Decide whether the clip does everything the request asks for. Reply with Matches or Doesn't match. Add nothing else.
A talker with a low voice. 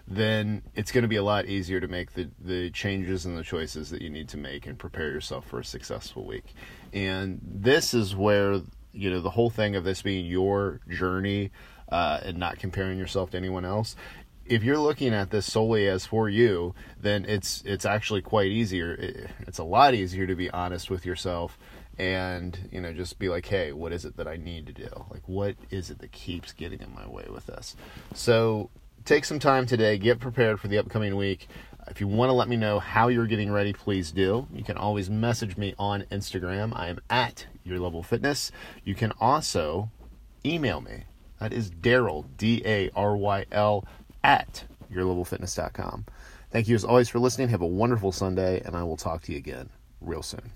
Matches